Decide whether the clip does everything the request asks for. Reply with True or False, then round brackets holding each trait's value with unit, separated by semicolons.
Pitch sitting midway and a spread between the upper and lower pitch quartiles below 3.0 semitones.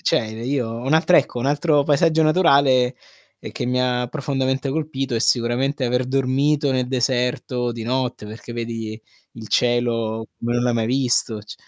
False (125 Hz; 2.6 semitones)